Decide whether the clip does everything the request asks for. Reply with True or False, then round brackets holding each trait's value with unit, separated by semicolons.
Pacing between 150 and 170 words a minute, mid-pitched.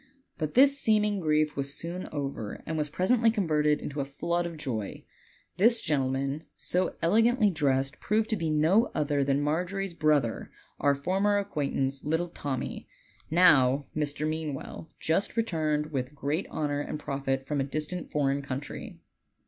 True (155 wpm; 150 Hz)